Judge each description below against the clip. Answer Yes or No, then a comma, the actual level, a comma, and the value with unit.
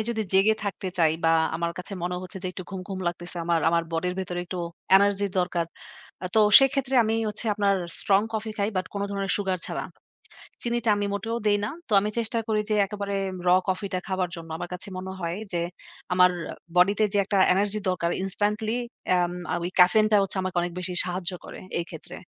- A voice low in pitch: No, high, 190 Hz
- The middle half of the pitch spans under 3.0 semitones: Yes, narrow, 2.6 semitones